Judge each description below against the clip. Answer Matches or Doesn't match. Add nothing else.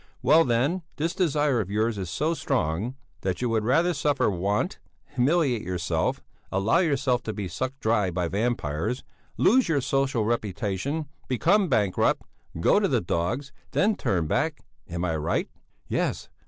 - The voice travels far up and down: Matches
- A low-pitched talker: Matches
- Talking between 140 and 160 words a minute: Matches